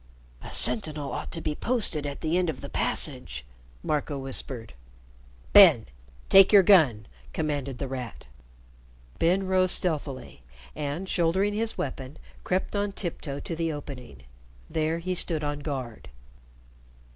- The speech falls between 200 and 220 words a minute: No, slow, 135 wpm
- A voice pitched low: No, medium, 150 Hz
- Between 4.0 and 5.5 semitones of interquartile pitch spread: Yes, average, 4.9 semitones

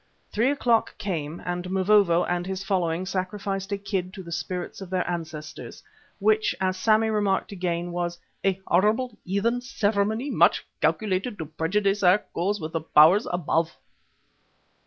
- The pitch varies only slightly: No, average, 3.1 semitones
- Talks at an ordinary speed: Yes, average, 145 wpm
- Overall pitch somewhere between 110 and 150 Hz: No, high, 190 Hz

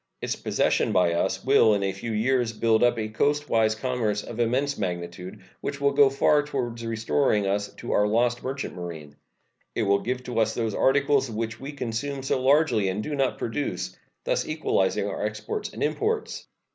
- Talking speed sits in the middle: Yes, average, 185 wpm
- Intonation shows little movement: No, average, 4.4 semitones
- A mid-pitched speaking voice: No, low, 115 Hz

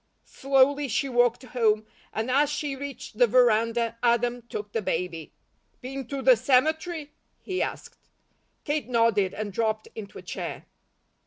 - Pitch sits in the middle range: No, high, 245 Hz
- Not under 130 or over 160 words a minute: Yes, average, 145 wpm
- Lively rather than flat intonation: No, average, 3.8 semitones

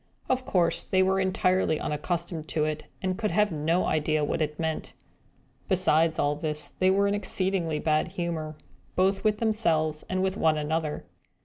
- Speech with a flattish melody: No, average, 3.5 semitones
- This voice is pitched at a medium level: Yes, medium, 170 Hz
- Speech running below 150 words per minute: No, average, 170 wpm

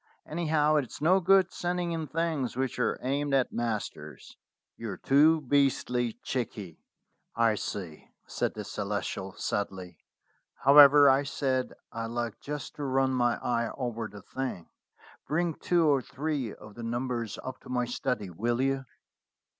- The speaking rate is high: No, average, 145 wpm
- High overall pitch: No, low, 130 Hz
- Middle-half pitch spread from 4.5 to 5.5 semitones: No, average, 4.0 semitones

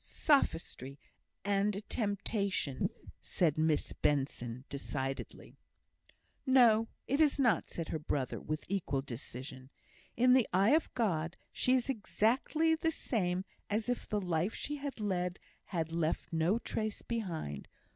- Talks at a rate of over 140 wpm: No, slow, 135 wpm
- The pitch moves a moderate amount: No, wide, 7.0 semitones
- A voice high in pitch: Yes, high, 195 Hz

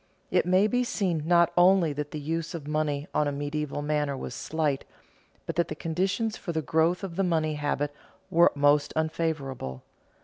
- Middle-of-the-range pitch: Yes, medium, 155 Hz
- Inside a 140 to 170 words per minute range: No, average, 180 wpm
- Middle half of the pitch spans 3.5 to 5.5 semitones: No, average, 2.8 semitones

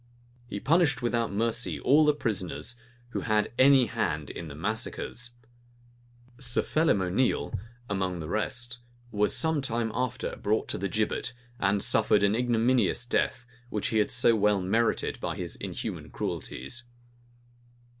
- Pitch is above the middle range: No, low, 115 Hz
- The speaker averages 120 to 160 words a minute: Yes, average, 145 wpm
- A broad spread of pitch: No, average, 3.3 semitones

